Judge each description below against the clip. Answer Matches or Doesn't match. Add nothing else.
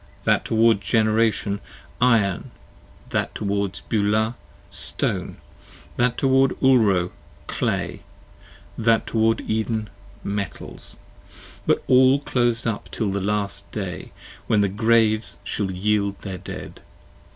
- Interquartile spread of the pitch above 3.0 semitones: Doesn't match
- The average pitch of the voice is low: Matches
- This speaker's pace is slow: Matches